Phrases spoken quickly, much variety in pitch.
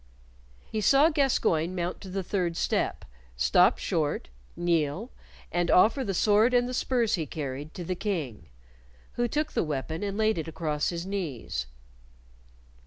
No: average, 155 wpm; wide, 5.7 semitones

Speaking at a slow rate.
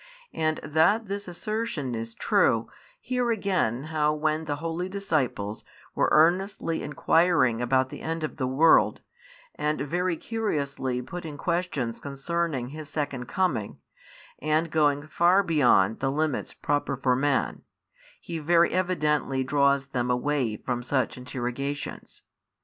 Yes: slow, 130 wpm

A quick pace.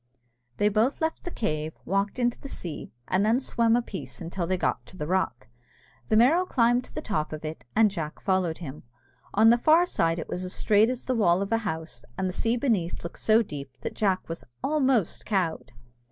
Yes: fast, 215 wpm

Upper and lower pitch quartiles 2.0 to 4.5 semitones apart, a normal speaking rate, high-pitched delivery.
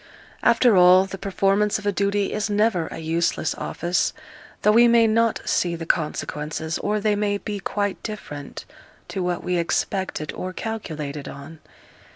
Yes: average, 4.1 semitones; average, 160 wpm; high, 195 Hz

